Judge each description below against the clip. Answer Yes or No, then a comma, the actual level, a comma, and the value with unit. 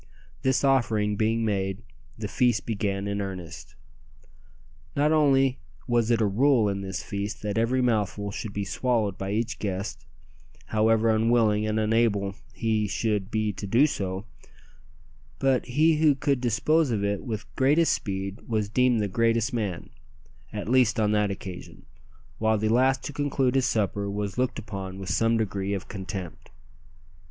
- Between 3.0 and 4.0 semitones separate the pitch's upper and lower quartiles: Yes, average, 3.4 semitones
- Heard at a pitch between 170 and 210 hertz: No, low, 110 Hz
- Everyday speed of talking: Yes, average, 160 wpm